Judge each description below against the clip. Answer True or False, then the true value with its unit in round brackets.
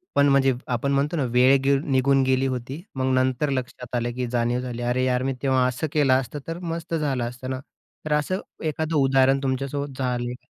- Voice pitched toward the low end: True (130 Hz)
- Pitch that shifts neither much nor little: False (2.0 semitones)